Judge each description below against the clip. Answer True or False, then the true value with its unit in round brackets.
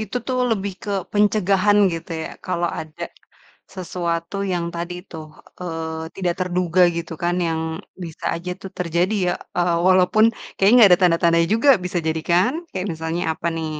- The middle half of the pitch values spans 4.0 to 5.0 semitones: False (2.5 semitones)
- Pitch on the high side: False (175 Hz)